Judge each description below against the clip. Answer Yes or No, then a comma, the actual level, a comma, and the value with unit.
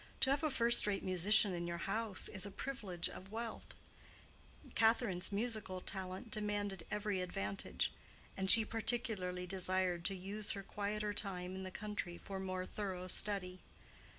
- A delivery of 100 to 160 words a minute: Yes, average, 150 wpm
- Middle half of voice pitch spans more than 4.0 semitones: No, narrow, 2.5 semitones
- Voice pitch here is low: No, high, 195 Hz